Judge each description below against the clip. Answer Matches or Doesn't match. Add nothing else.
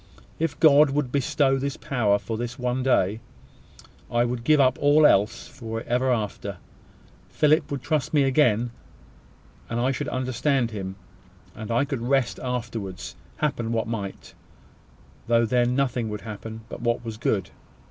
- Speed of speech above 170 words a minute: Doesn't match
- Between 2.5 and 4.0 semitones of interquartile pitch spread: Matches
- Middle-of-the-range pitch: Doesn't match